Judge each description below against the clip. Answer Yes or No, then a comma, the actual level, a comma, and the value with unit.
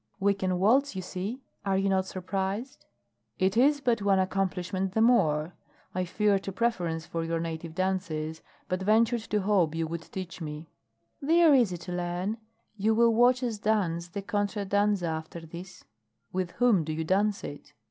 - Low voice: No, high, 190 Hz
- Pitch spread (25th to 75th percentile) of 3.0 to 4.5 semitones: Yes, average, 3.7 semitones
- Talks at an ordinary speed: Yes, average, 180 wpm